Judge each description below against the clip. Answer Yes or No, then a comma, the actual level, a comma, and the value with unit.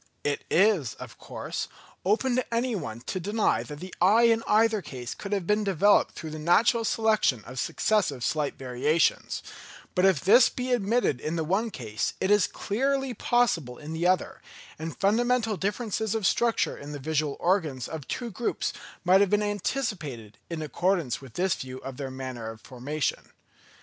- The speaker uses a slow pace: No, average, 175 wpm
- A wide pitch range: Yes, wide, 7.2 semitones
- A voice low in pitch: No, medium, 185 Hz